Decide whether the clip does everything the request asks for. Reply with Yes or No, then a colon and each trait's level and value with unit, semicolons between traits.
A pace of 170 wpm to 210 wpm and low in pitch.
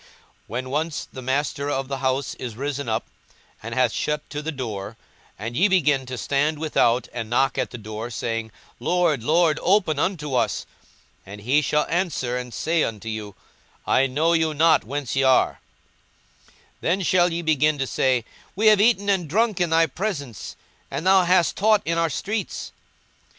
No: average, 185 wpm; medium, 145 Hz